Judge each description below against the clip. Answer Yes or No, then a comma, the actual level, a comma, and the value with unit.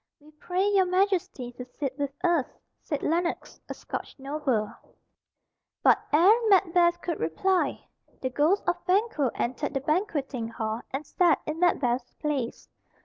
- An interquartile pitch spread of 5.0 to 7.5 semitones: Yes, wide, 5.5 semitones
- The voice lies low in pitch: No, very high, 305 Hz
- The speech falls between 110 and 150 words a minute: Yes, average, 145 wpm